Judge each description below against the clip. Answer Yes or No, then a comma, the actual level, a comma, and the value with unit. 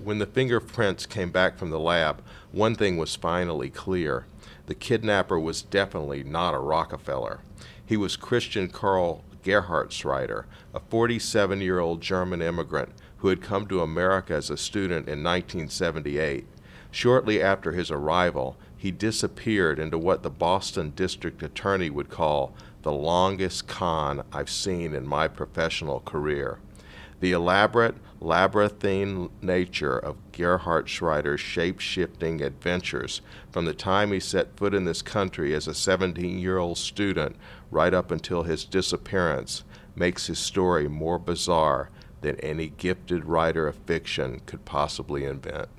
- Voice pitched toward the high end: No, very low, 90 Hz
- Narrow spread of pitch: No, average, 3.2 semitones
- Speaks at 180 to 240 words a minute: No, average, 140 wpm